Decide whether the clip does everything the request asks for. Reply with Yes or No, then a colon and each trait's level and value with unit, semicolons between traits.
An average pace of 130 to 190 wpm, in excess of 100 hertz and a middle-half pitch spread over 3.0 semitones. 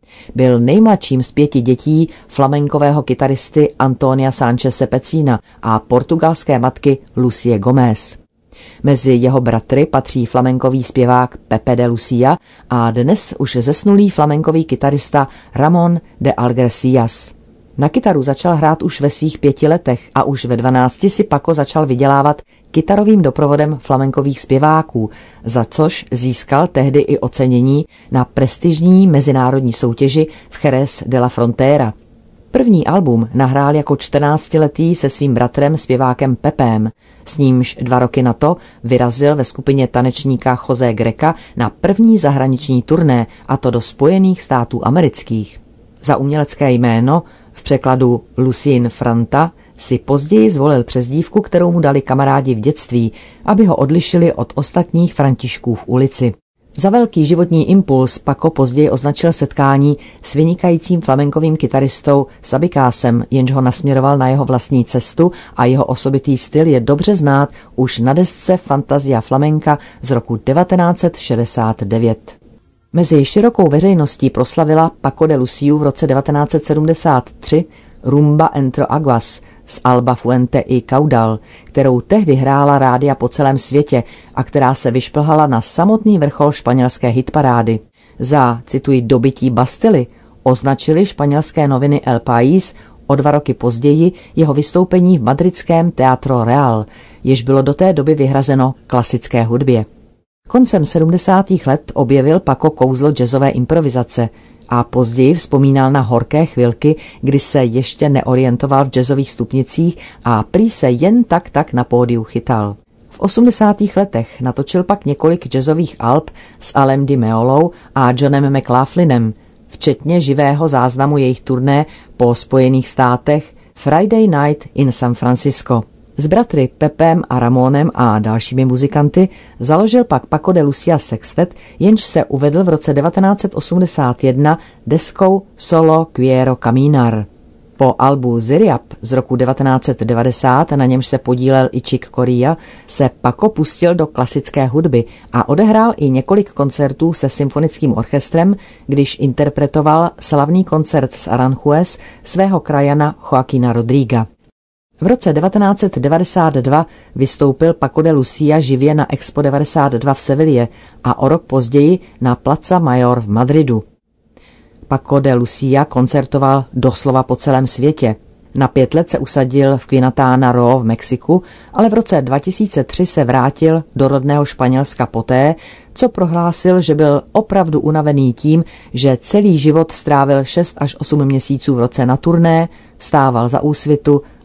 Yes: average, 135 wpm; medium, 140 Hz; average, 3.6 semitones